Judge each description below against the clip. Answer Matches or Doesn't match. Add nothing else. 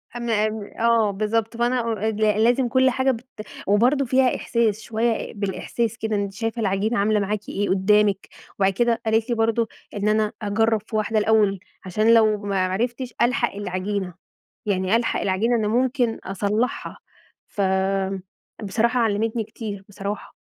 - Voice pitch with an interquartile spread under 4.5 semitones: Matches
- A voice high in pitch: Matches